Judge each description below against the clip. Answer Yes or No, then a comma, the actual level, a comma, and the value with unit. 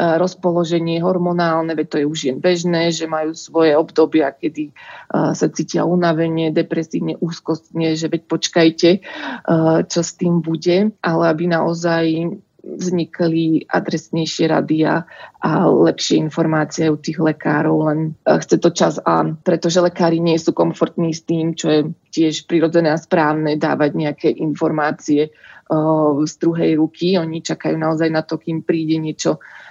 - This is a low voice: No, medium, 165 Hz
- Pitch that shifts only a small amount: Yes, narrow, 1.3 semitones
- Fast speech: No, average, 140 wpm